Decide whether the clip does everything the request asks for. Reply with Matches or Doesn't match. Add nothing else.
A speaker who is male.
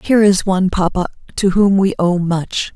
Doesn't match